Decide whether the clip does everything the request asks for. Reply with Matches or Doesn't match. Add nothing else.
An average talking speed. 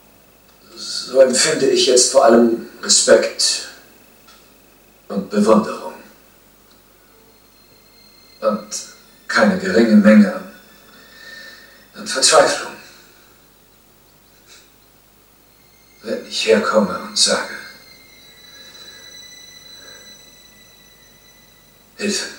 Doesn't match